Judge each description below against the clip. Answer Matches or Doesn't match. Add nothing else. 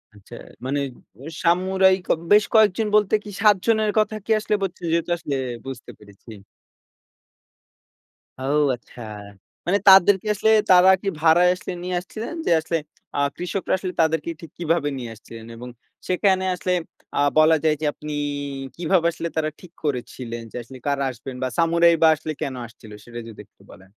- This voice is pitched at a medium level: Matches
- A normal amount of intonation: Doesn't match